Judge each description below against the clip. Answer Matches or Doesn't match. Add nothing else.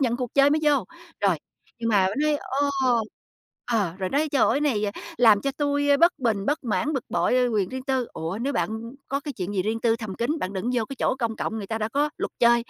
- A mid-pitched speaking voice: Doesn't match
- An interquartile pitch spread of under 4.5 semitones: Doesn't match